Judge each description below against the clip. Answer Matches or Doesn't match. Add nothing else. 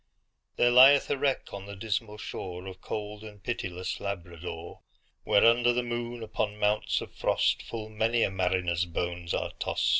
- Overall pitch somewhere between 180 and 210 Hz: Doesn't match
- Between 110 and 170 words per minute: Matches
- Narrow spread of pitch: Doesn't match